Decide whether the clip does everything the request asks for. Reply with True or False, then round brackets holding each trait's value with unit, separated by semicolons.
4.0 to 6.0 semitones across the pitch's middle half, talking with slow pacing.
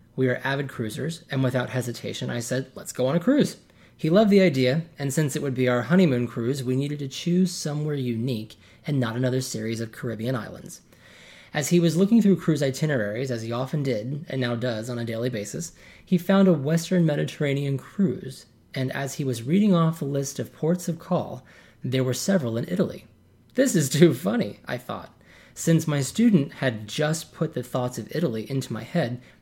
False (4.9 semitones; 200 wpm)